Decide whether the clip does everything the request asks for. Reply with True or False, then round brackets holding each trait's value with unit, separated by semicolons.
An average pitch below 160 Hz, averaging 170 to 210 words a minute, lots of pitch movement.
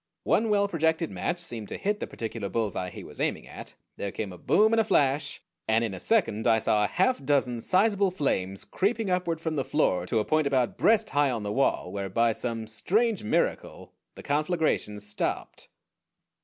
True (140 Hz; 195 wpm; 9.0 semitones)